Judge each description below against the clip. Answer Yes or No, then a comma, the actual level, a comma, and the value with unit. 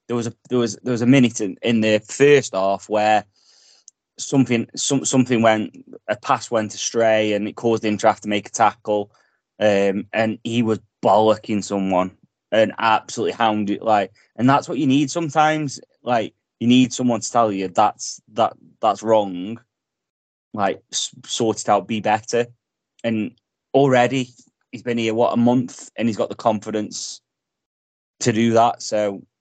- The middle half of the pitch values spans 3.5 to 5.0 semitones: No, narrow, 2.5 semitones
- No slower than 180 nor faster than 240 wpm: No, average, 165 wpm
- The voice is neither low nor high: No, low, 110 Hz